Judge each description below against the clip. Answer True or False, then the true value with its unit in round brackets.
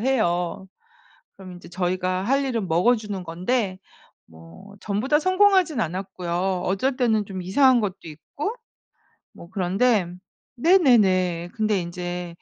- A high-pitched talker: True (195 Hz)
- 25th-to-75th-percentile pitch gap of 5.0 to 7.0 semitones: True (5.6 semitones)